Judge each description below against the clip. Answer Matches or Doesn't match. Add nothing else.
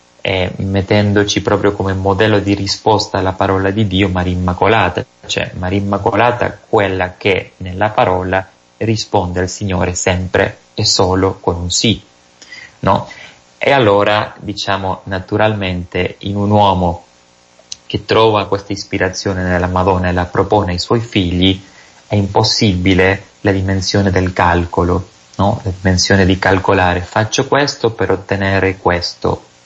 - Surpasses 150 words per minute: Doesn't match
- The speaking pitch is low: Matches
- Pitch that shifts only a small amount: Matches